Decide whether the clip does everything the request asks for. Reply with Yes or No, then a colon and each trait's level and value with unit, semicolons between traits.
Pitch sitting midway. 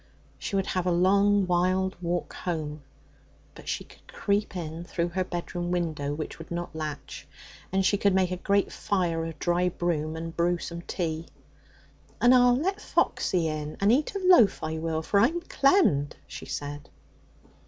Yes: medium, 175 Hz